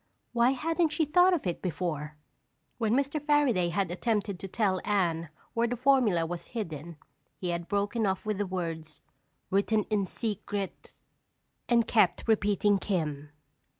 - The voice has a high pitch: Yes, high, 205 Hz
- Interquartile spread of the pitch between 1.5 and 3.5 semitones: No, average, 5.2 semitones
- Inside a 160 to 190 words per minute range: No, average, 150 wpm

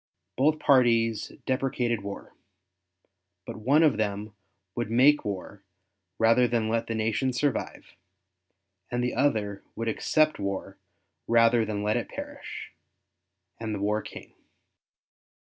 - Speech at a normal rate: No, slow, 125 wpm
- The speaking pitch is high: No, low, 115 Hz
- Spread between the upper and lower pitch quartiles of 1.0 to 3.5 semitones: Yes, average, 2.9 semitones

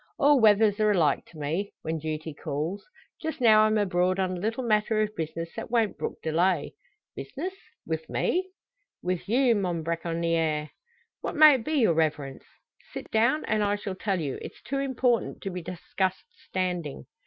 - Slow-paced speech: No, average, 175 wpm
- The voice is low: No, high, 190 Hz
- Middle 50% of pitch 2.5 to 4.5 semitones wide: No, average, 5.2 semitones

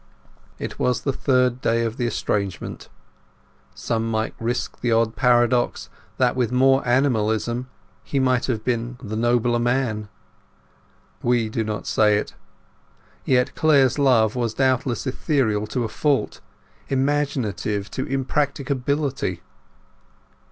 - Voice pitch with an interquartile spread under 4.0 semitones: Yes, average, 2.9 semitones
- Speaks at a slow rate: Yes, slow, 125 wpm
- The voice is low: Yes, low, 120 Hz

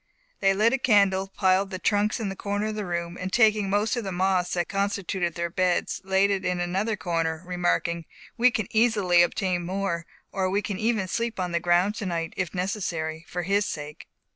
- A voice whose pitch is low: No, high, 190 Hz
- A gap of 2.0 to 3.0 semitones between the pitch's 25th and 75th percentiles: Yes, average, 2.7 semitones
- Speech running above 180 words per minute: Yes, average, 200 wpm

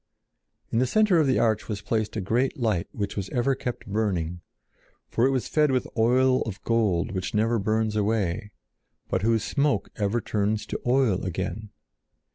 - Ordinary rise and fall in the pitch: Yes, average, 3.4 semitones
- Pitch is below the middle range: Yes, low, 110 Hz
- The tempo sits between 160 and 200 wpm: Yes, average, 175 wpm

